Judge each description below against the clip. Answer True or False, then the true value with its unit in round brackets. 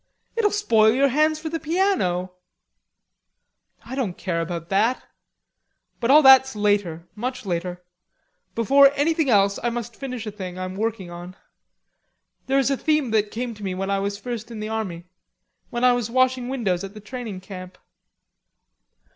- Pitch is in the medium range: False (220 Hz)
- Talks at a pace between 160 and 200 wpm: True (170 wpm)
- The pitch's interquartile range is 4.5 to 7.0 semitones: True (5.4 semitones)